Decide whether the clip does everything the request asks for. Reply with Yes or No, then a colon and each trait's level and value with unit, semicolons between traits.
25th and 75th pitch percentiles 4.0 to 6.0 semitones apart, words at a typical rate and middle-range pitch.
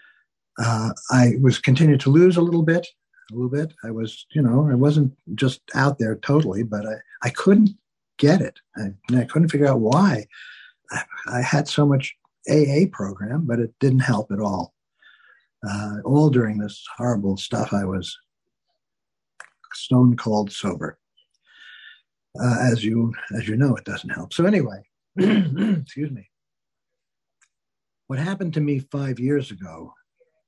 No: average, 5.1 semitones; average, 155 wpm; low, 130 Hz